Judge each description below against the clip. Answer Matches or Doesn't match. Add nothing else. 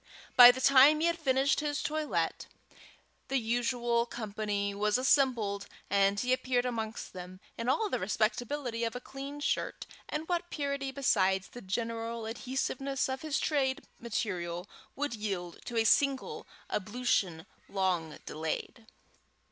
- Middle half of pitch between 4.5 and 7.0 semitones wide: Matches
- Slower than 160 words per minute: Matches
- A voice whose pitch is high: Matches